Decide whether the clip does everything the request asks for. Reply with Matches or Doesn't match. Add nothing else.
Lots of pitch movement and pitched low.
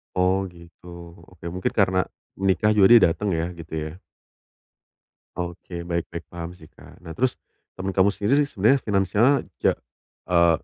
Doesn't match